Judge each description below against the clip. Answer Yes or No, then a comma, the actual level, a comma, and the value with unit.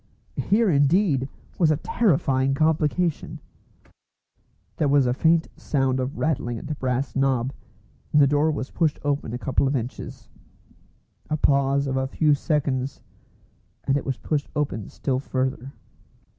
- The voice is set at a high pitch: No, medium, 140 Hz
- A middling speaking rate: Yes, average, 145 wpm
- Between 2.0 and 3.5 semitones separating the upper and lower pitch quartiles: Yes, narrow, 2.6 semitones